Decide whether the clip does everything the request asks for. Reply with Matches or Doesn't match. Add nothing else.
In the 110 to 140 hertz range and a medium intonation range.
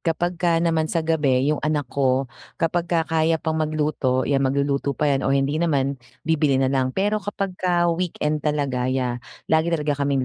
Doesn't match